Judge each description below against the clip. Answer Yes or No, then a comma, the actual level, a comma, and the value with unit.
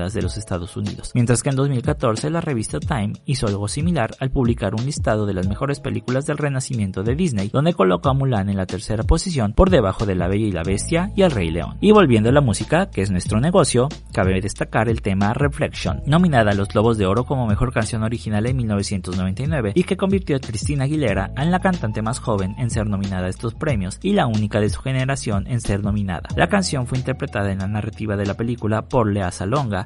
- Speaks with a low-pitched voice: Yes, low, 115 Hz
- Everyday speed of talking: No, fast, 225 wpm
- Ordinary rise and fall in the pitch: No, wide, 5.7 semitones